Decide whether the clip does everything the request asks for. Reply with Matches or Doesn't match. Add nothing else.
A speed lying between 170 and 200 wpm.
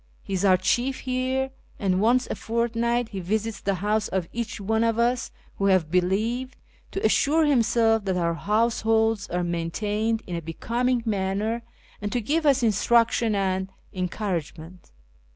Doesn't match